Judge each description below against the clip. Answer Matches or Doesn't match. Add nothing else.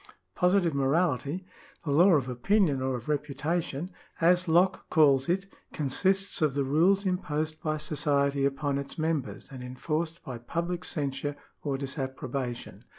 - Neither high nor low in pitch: Matches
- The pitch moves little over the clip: Doesn't match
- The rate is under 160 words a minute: Matches